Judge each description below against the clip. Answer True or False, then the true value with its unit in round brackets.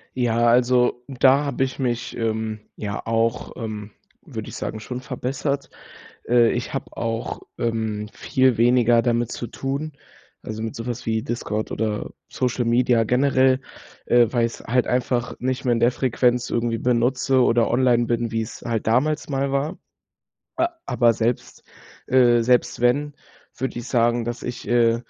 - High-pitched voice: False (120 Hz)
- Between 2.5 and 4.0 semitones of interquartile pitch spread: False (1.8 semitones)